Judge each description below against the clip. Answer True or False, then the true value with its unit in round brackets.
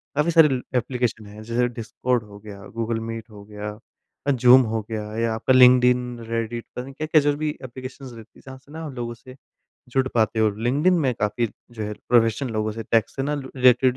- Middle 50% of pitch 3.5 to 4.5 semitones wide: False (2.7 semitones)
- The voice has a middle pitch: False (120 Hz)